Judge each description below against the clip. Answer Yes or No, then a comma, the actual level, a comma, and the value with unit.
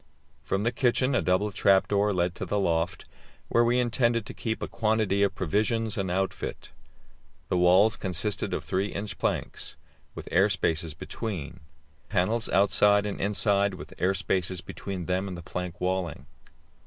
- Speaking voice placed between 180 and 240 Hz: No, low, 100 Hz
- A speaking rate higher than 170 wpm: No, average, 165 wpm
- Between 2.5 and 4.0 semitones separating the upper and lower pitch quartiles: Yes, average, 2.8 semitones